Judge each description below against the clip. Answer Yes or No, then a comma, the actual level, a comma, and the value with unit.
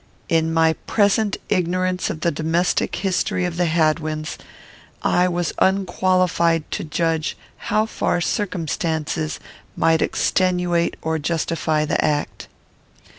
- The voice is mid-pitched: Yes, medium, 170 Hz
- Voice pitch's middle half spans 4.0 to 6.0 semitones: No, narrow, 2.4 semitones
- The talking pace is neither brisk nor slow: No, slow, 115 wpm